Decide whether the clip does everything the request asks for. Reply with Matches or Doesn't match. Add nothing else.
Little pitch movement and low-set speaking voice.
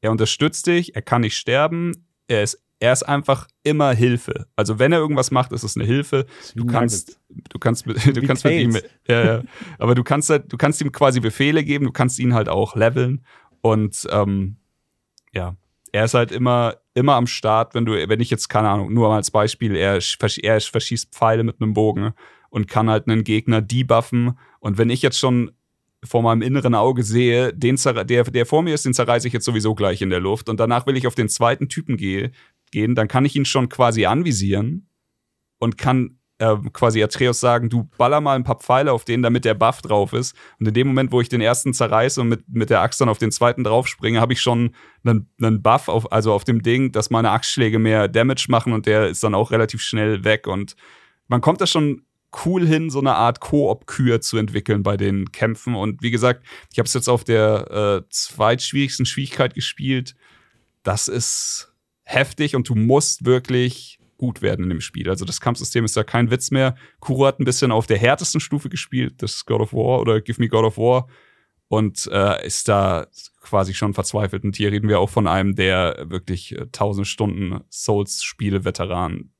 Doesn't match